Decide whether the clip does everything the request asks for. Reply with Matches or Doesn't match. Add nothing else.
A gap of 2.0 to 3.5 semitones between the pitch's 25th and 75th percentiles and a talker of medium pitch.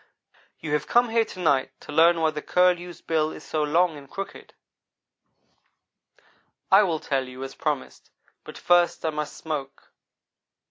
Matches